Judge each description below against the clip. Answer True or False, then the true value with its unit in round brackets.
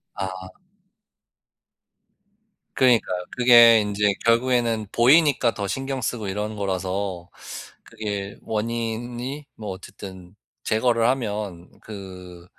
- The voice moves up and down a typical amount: True (3.6 semitones)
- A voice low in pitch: True (105 Hz)